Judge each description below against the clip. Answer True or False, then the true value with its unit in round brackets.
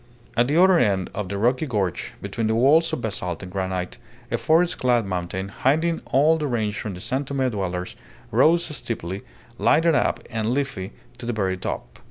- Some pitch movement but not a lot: False (6.7 semitones)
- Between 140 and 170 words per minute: False (190 wpm)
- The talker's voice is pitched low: True (115 Hz)